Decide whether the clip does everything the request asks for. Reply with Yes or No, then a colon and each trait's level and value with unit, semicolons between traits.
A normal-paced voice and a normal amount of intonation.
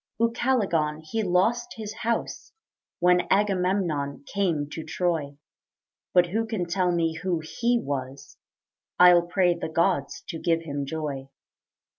No: slow, 130 wpm; average, 4.1 semitones